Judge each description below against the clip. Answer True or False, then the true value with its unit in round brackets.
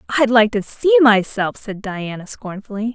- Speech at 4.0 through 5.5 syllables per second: True (4.7 syllables/s)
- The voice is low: False (220 Hz)